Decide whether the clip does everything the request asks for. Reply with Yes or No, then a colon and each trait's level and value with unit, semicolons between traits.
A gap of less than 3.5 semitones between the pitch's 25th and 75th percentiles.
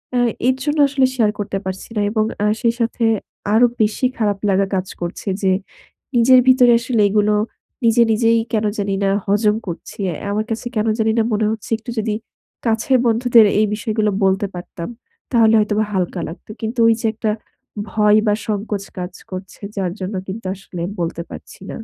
Yes: average, 2.7 semitones